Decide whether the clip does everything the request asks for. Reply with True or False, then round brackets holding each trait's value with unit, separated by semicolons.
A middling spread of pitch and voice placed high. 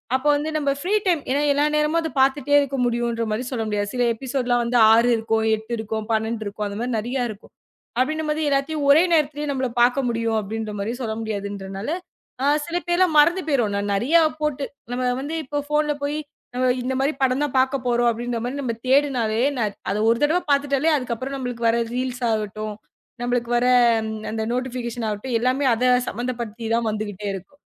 True (4.0 semitones; 245 Hz)